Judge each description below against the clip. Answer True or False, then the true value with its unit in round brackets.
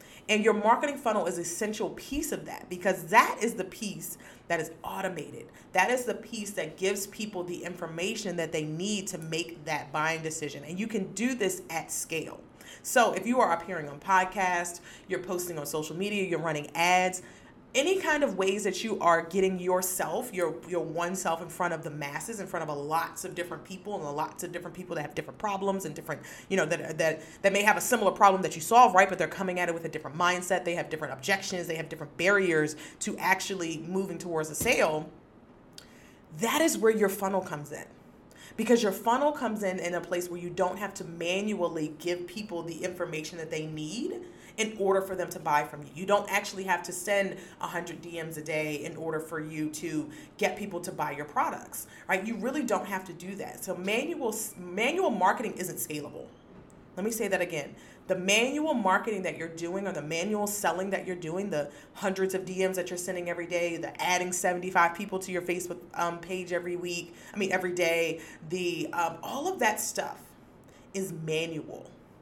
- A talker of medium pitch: True (180 Hz)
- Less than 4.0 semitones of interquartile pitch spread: True (3.0 semitones)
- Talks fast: True (210 wpm)